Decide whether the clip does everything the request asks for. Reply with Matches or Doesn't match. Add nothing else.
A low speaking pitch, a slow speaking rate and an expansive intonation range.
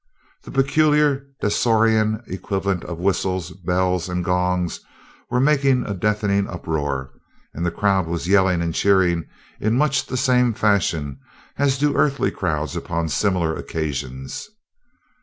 Matches